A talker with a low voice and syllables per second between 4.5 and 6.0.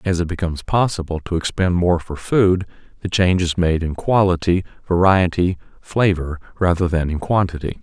Yes: very low, 90 Hz; 5.2 syllables/s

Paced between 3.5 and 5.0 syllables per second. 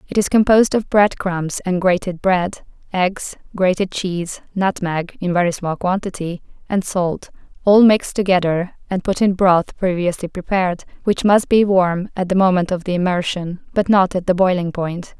Yes: 4.5 syllables/s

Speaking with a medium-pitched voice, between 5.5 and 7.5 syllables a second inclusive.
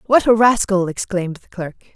No: high, 200 Hz; 5.7 syllables/s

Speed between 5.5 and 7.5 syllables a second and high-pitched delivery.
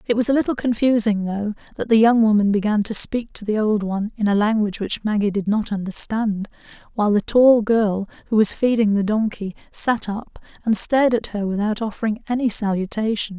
Yes: 5.6 syllables/s; high, 215 Hz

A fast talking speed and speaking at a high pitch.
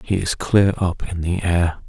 No: fast, 225 wpm; very low, 90 Hz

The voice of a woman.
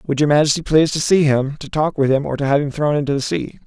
No: male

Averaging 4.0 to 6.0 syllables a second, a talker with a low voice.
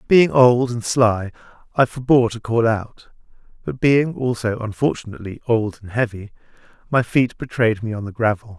Yes: 5.0 syllables/s; low, 115 Hz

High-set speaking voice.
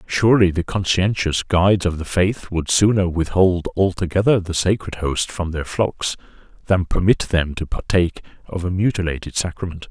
No: very low, 90 Hz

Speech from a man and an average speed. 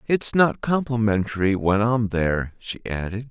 Yes: male; average, 145 wpm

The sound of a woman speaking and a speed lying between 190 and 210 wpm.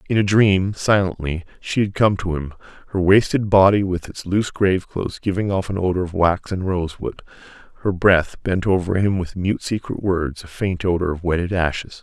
No: male; average, 195 wpm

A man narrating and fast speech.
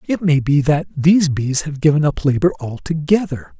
No: male; average, 185 wpm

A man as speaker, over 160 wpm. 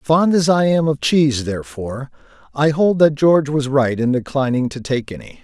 Yes: male; average, 200 wpm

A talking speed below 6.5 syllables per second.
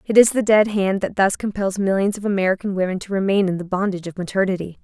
No: 6.6 syllables/s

